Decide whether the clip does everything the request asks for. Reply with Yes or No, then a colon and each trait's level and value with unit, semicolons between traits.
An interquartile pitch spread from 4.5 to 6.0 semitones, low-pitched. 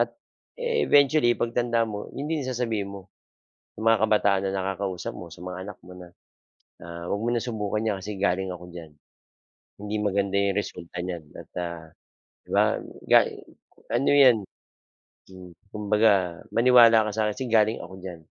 No: average, 3.9 semitones; low, 105 Hz